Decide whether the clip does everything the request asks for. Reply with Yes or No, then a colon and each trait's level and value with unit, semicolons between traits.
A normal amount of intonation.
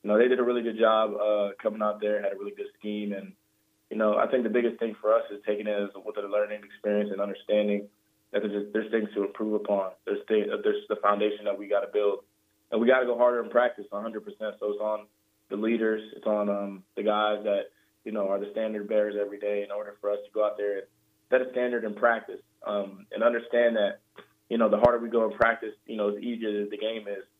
No: narrow, 1.7 semitones